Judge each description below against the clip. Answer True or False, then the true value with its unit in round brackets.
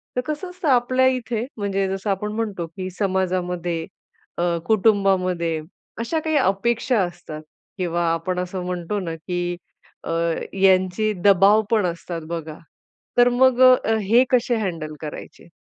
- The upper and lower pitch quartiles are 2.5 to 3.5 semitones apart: False (4.8 semitones)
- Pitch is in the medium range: False (195 Hz)